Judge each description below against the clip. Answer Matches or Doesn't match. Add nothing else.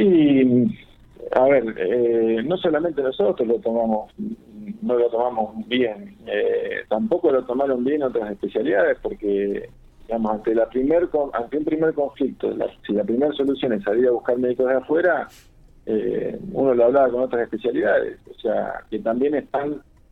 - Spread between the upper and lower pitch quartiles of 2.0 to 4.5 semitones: Doesn't match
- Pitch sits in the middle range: Doesn't match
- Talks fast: Doesn't match